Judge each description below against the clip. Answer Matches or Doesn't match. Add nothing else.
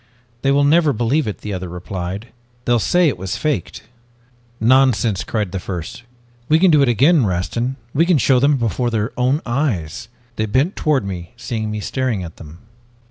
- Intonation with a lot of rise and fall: Matches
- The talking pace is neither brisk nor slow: Matches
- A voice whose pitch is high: Doesn't match